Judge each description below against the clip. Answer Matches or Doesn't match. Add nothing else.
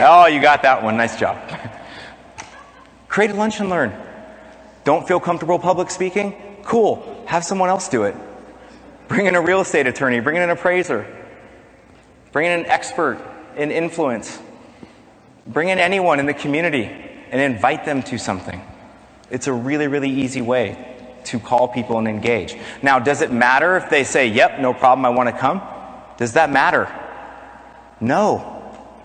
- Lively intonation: Matches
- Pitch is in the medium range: Matches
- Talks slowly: Doesn't match